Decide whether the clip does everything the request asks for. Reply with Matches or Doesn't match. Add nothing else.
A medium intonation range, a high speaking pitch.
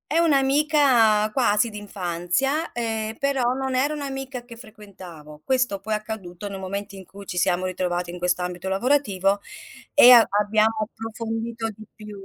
Matches